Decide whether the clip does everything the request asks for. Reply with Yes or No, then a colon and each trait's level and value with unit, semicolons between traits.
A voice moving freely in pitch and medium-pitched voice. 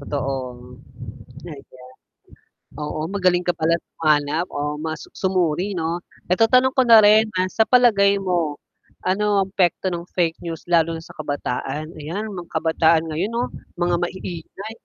No: average, 3.8 semitones; medium, 170 Hz